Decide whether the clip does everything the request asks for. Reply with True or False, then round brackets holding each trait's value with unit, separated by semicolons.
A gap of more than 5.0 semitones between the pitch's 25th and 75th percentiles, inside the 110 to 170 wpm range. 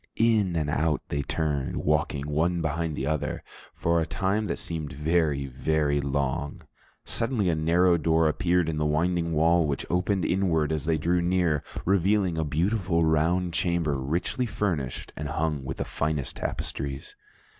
False (3.0 semitones; 160 wpm)